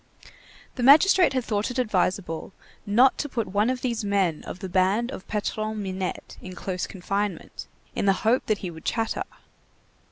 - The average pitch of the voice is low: No, high, 205 Hz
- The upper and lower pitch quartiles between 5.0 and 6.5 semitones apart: No, average, 4.1 semitones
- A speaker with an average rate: Yes, average, 170 wpm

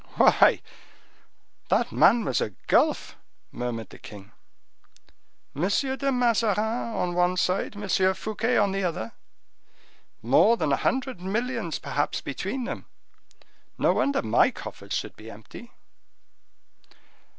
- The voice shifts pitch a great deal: Yes, wide, 8.8 semitones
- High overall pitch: Yes, high, 195 Hz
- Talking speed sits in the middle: No, slow, 115 wpm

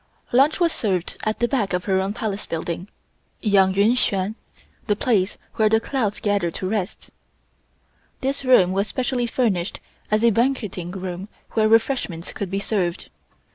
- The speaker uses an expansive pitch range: No, average, 3.8 semitones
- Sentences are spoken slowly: No, average, 160 wpm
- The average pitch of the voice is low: No, high, 205 Hz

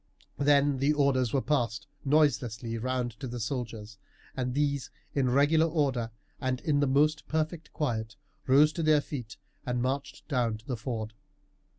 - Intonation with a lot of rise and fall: No, average, 3.3 semitones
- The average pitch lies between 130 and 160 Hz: Yes, low, 135 Hz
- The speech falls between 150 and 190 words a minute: Yes, average, 160 wpm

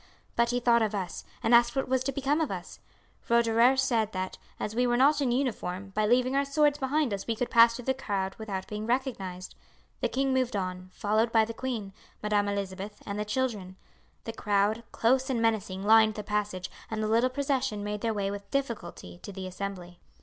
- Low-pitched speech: No, high, 225 Hz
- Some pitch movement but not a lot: Yes, average, 4.1 semitones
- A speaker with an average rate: No, fast, 210 wpm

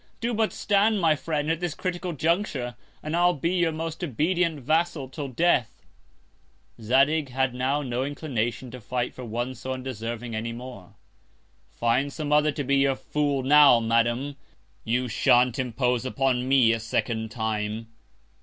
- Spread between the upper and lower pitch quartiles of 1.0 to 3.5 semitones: No, average, 4.4 semitones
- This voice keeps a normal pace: Yes, average, 155 wpm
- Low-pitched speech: Yes, low, 130 Hz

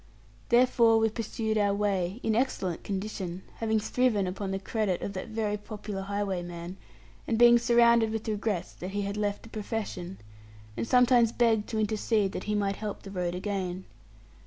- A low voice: No, high, 210 Hz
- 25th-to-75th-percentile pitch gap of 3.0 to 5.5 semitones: No, narrow, 2.6 semitones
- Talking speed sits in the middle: Yes, average, 170 wpm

